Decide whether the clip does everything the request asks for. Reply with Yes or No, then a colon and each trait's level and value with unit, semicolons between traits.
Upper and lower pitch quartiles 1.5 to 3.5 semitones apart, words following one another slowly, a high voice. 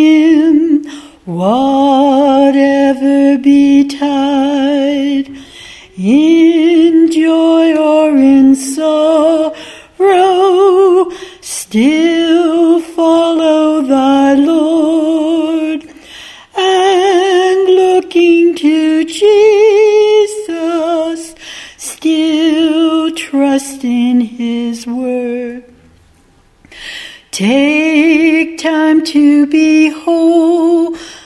Yes: average, 3.1 semitones; slow, 50 wpm; very high, 315 Hz